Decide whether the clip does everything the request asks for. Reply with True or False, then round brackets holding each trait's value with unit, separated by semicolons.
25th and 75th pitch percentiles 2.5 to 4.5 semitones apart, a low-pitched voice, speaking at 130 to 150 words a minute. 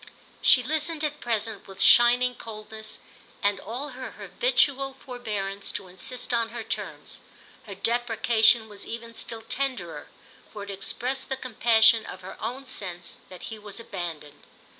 False (3.7 semitones; 225 Hz; 145 wpm)